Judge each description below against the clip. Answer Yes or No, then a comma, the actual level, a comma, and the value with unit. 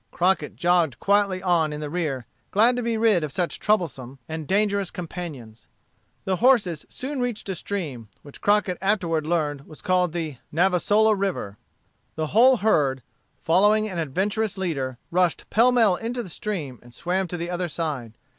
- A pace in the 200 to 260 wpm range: No, average, 165 wpm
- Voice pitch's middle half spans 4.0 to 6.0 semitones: Yes, average, 5.0 semitones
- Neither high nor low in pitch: Yes, medium, 180 Hz